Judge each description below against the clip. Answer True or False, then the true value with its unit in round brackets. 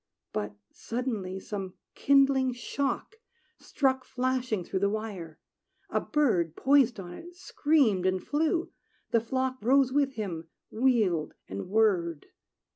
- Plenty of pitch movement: True (6.2 semitones)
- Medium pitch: False (230 Hz)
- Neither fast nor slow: False (120 wpm)